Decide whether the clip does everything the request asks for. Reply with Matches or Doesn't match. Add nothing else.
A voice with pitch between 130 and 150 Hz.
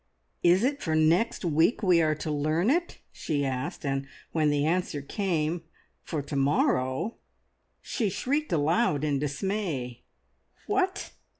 Doesn't match